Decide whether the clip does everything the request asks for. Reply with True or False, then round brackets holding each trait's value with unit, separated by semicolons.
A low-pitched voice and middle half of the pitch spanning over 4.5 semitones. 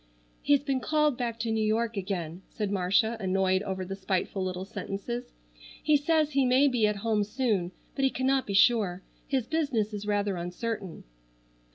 False (215 Hz; 4.9 semitones)